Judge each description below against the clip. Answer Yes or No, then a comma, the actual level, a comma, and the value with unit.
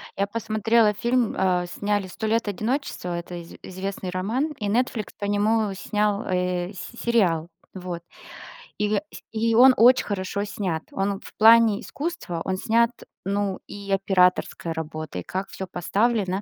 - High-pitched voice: Yes, high, 200 Hz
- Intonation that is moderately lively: Yes, average, 3.6 semitones